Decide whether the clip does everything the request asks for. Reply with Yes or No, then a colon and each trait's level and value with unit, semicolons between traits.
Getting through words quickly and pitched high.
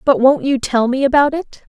Yes: fast, 240 wpm; very high, 260 Hz